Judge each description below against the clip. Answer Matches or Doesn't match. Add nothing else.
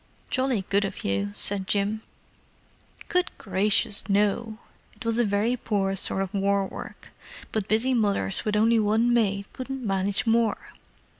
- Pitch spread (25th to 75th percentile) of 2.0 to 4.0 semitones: Matches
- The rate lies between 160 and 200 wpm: Doesn't match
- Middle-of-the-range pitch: Doesn't match